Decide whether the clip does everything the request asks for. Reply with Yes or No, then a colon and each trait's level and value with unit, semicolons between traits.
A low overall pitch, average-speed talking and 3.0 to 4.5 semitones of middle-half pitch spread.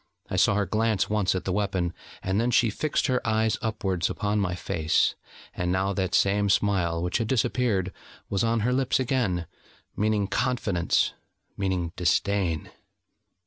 Yes: low, 100 Hz; average, 155 wpm; average, 3.4 semitones